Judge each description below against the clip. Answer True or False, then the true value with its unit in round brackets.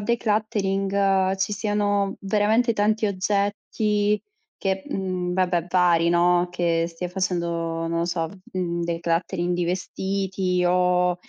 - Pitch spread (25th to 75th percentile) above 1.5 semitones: True (2.5 semitones)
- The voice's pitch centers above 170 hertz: True (185 Hz)